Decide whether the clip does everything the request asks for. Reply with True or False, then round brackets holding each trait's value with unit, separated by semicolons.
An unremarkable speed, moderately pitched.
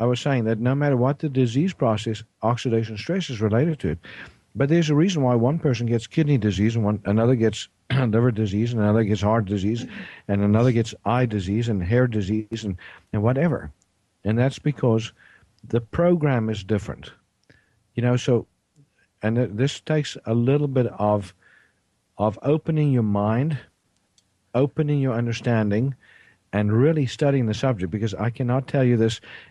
False (170 wpm; 115 Hz)